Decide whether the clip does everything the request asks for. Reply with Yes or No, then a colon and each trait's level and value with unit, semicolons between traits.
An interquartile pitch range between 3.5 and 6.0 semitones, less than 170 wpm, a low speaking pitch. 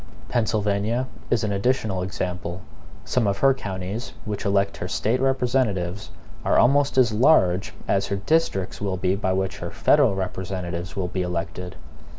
Yes: average, 4.5 semitones; average, 155 wpm; low, 100 Hz